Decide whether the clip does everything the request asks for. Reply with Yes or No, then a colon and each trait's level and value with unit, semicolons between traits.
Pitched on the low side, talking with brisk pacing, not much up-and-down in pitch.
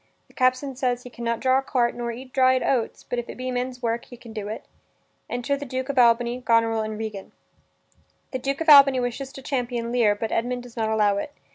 No: high, 245 Hz; fast, 235 wpm; narrow, 2.0 semitones